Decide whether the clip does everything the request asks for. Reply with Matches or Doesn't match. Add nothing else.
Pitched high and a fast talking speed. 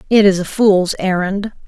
Doesn't match